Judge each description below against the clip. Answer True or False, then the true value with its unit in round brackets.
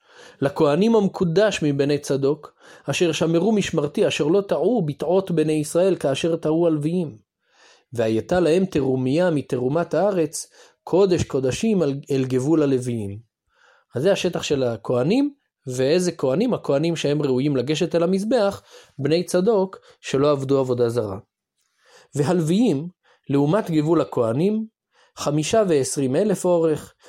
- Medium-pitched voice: True (155 Hz)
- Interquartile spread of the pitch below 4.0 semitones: False (4.6 semitones)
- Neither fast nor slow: True (120 wpm)